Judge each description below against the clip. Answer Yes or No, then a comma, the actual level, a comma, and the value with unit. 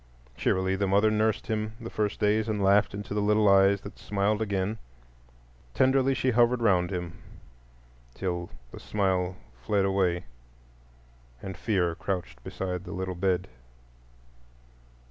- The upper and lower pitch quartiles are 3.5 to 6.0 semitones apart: No, narrow, 2.6 semitones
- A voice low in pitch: Yes, low, 100 Hz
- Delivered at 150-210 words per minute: No, average, 140 wpm